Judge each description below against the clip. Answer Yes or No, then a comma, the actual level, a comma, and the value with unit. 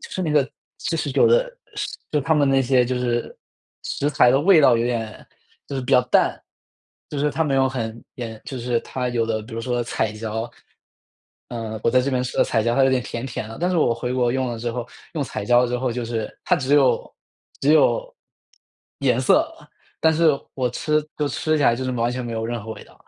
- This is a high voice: No, low, 125 Hz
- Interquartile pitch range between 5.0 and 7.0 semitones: No, average, 3.2 semitones